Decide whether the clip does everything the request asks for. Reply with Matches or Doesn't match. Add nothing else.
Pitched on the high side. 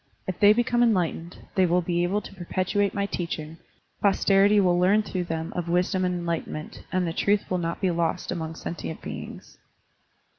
Doesn't match